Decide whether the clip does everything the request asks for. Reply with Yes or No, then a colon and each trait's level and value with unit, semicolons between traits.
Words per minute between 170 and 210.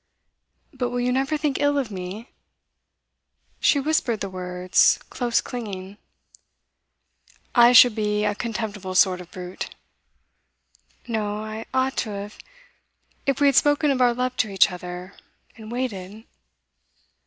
No: slow, 135 wpm